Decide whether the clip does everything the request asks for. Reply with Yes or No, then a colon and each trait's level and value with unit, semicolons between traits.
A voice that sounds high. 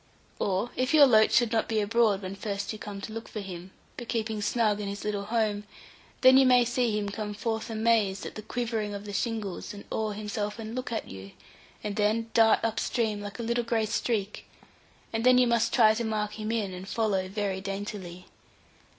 Yes: high, 215 Hz